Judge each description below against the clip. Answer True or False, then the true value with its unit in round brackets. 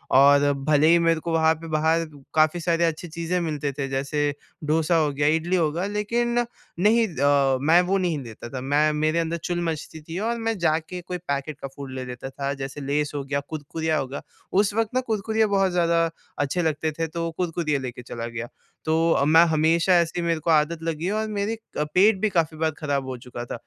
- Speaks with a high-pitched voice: False (160 Hz)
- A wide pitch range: False (3.5 semitones)